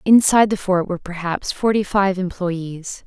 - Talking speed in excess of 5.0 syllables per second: No, 4.8 syllables/s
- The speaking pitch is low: No, medium, 185 Hz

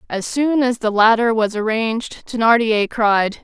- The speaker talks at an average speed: Yes, average, 155 wpm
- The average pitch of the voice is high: Yes, high, 225 Hz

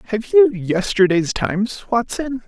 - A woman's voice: No, male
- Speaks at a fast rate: No, slow, 120 wpm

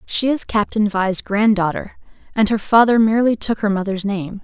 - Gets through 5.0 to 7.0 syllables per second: Yes, 5.1 syllables/s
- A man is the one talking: No, female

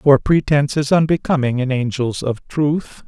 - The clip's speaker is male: Yes, male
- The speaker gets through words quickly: No, average, 155 wpm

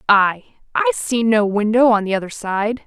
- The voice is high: Yes, high, 210 Hz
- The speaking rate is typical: Yes, average, 170 wpm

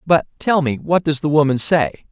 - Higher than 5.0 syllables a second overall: No, 4.9 syllables/s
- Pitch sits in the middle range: Yes, medium, 150 Hz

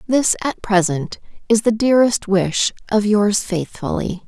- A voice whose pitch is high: Yes, high, 210 Hz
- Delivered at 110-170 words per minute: Yes, average, 140 wpm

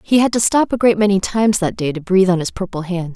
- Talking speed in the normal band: No, fast, 305 wpm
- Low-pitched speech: No, high, 195 Hz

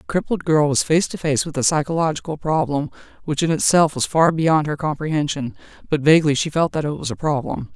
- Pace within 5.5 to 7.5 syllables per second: Yes, 6.0 syllables/s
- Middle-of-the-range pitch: Yes, medium, 155 Hz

